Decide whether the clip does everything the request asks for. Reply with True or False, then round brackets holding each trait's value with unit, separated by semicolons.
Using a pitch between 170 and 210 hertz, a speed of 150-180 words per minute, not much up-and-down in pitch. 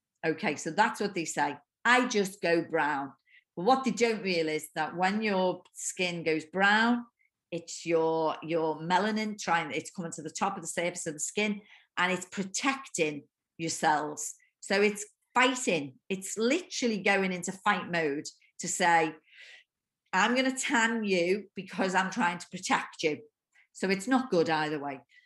False (190 Hz; 165 wpm; 5.2 semitones)